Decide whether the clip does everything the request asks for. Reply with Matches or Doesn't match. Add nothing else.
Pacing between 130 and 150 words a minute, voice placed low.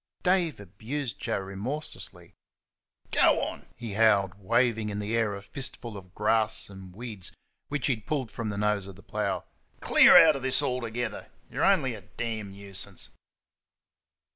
Doesn't match